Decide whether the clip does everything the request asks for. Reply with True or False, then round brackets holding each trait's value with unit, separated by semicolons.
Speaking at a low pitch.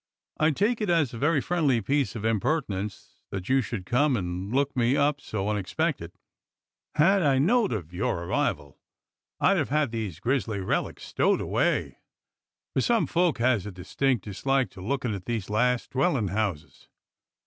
True (125 Hz)